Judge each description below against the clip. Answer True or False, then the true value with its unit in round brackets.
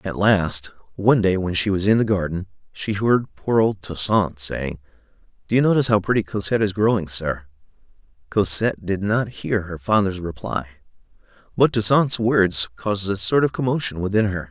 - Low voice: True (100 Hz)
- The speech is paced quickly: False (175 wpm)